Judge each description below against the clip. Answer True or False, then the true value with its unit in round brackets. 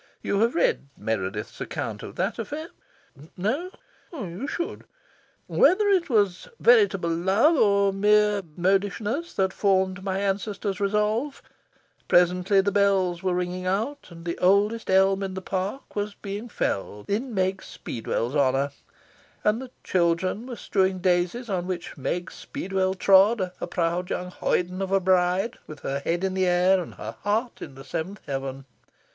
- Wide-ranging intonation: False (2.8 semitones)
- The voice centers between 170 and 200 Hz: True (190 Hz)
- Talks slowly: False (155 wpm)